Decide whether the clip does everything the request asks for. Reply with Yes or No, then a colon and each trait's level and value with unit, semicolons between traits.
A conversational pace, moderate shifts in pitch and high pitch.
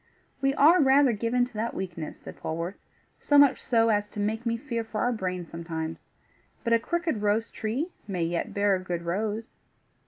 Yes: average, 190 wpm; average, 5.0 semitones; high, 220 Hz